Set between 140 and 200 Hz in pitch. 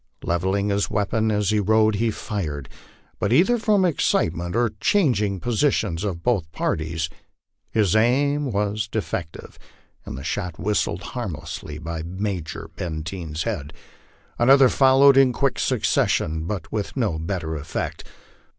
No: low, 100 Hz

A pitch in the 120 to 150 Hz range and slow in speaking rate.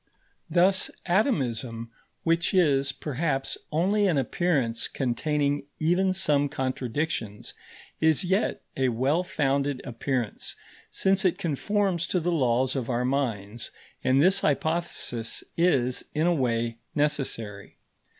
Yes: medium, 140 Hz; slow, 115 wpm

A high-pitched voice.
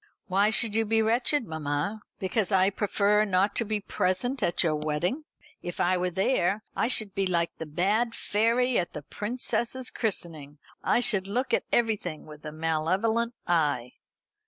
Yes: high, 200 Hz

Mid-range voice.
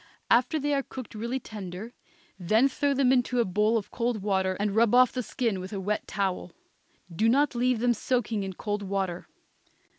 No: high, 225 Hz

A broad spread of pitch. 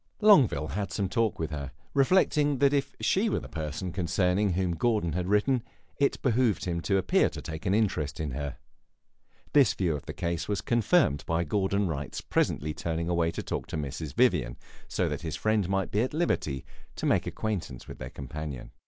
Yes: wide, 6.2 semitones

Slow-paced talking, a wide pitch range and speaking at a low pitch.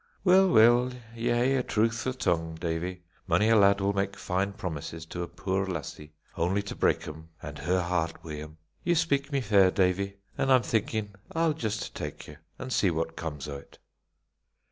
No: average, 185 wpm; wide, 5.9 semitones; low, 100 Hz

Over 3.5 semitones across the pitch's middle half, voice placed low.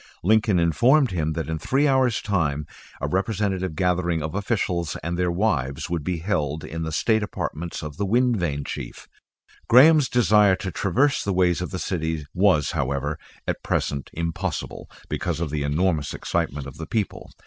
Yes: average, 4.9 semitones; very low, 90 Hz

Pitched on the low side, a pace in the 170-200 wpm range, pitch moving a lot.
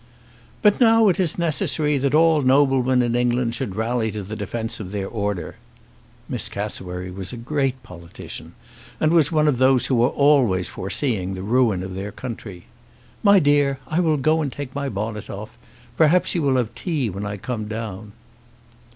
Yes: low, 125 Hz; average, 180 wpm; wide, 5.9 semitones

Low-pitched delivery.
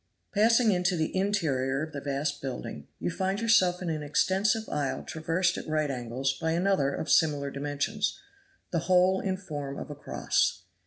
No: medium, 160 Hz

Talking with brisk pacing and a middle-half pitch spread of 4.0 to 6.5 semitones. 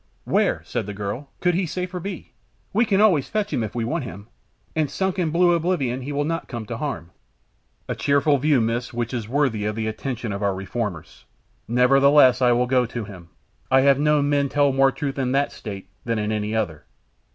Yes: fast, 210 wpm; average, 5.0 semitones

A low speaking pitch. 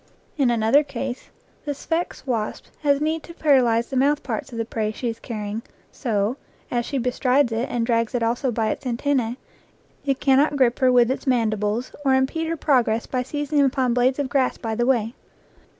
No: very high, 250 Hz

